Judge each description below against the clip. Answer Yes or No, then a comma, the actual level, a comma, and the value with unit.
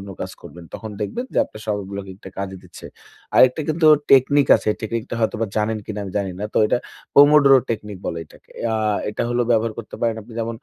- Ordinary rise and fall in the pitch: Yes, average, 3.4 semitones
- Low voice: Yes, low, 110 Hz